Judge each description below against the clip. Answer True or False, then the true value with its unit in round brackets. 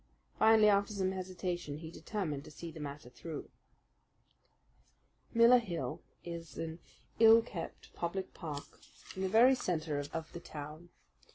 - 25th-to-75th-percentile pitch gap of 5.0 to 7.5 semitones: False (4.3 semitones)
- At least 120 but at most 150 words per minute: True (140 wpm)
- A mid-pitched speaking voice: True (175 Hz)